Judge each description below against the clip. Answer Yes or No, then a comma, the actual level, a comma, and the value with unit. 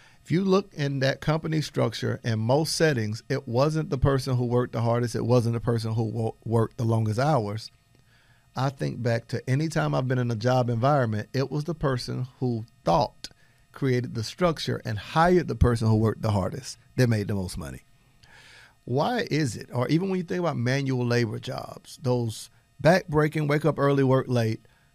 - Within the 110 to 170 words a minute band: No, average, 190 wpm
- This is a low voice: Yes, low, 125 Hz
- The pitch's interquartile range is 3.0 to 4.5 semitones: Yes, average, 3.6 semitones